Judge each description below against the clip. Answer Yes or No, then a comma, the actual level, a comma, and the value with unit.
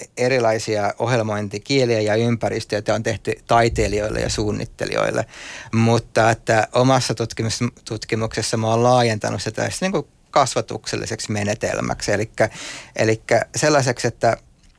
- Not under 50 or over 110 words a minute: Yes, slow, 95 wpm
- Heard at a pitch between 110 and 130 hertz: Yes, low, 115 Hz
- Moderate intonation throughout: No, narrow, 1.6 semitones